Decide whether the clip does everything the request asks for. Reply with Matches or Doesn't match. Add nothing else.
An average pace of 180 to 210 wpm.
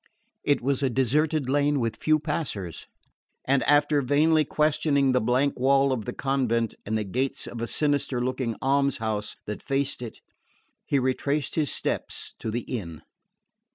Doesn't match